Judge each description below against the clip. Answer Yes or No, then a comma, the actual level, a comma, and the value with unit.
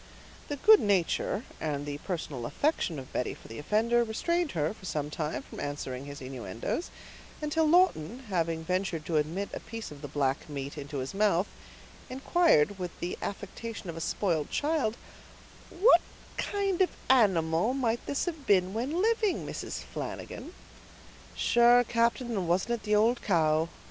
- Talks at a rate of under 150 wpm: No, average, 160 wpm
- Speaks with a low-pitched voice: No, high, 195 Hz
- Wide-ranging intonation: Yes, wide, 8.1 semitones